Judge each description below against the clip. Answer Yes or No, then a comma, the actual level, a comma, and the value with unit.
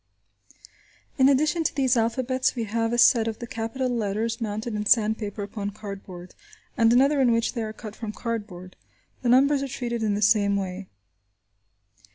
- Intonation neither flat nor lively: Yes, average, 3.0 semitones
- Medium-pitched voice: No, high, 225 Hz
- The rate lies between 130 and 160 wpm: No, average, 175 wpm